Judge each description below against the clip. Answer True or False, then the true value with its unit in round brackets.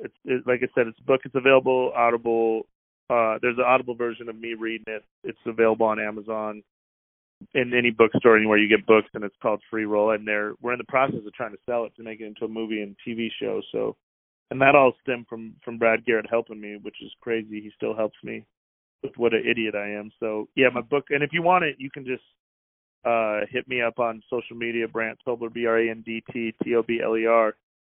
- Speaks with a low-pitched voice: True (115 Hz)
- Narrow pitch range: True (2.0 semitones)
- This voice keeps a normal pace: False (245 wpm)